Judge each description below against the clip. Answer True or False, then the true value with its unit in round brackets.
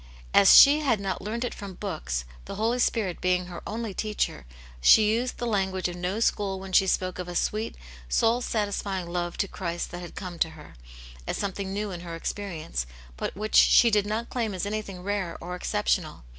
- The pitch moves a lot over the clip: False (3.2 semitones)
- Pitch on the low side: False (195 Hz)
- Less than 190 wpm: False (205 wpm)